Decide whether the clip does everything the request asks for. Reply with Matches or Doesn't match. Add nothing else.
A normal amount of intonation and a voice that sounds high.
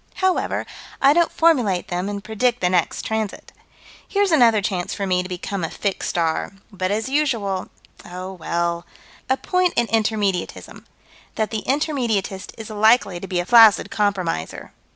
Matches